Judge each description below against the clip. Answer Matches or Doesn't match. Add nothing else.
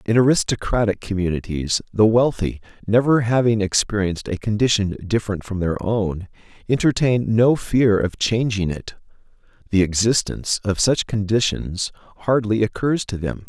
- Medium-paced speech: Doesn't match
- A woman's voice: Doesn't match